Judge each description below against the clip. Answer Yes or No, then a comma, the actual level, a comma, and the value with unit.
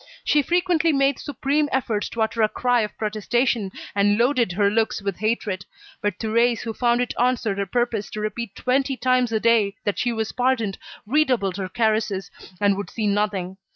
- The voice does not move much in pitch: No, average, 3.3 semitones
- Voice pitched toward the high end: Yes, high, 225 Hz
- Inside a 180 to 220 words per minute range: Yes, average, 185 wpm